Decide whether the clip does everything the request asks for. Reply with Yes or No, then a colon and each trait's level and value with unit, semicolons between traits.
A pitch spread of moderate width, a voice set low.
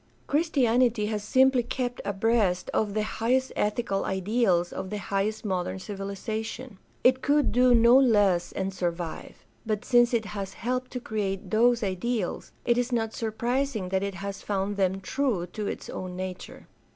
No: average, 4.0 semitones; high, 215 Hz